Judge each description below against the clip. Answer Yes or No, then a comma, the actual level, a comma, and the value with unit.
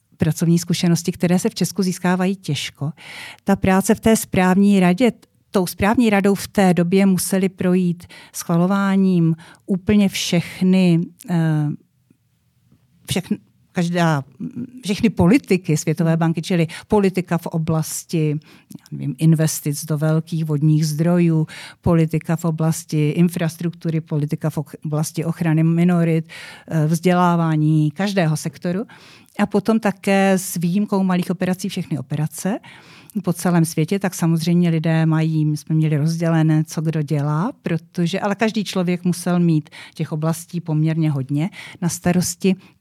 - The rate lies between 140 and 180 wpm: No, average, 125 wpm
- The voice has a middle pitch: Yes, medium, 170 Hz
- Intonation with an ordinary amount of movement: Yes, average, 3.0 semitones